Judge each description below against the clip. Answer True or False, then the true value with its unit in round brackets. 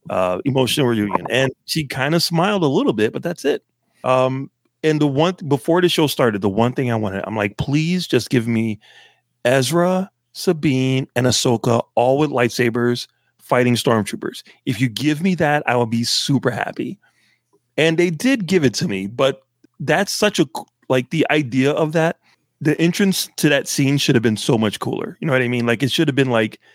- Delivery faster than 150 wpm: True (205 wpm)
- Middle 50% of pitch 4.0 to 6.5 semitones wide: True (4.9 semitones)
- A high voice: False (135 Hz)